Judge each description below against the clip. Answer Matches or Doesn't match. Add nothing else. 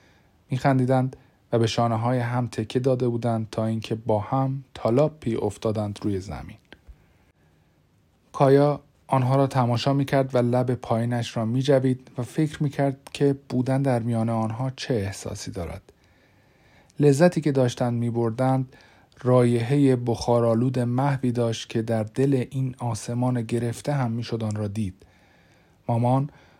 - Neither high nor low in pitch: Doesn't match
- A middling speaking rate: Matches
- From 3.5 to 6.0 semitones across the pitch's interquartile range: Doesn't match